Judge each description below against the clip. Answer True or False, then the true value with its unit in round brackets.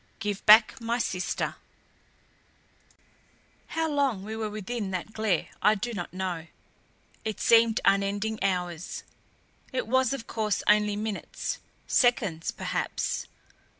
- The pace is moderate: False (115 wpm)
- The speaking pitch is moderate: False (215 Hz)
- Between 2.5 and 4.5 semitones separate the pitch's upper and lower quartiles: True (2.9 semitones)